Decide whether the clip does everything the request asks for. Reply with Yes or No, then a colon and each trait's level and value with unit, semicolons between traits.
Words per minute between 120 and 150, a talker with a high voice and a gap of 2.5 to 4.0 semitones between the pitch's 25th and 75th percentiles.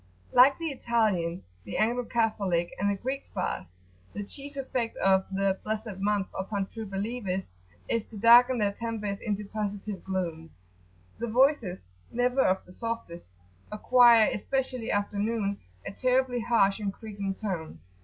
Yes: average, 145 wpm; high, 210 Hz; average, 3.4 semitones